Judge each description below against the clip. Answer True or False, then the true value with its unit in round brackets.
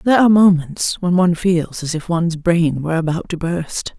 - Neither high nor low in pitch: True (170 Hz)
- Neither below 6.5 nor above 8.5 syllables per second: False (5.4 syllables/s)